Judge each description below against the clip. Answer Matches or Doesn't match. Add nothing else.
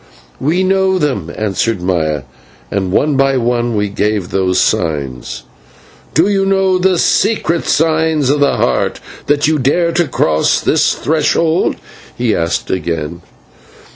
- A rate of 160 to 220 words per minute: Doesn't match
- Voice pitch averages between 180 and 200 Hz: Doesn't match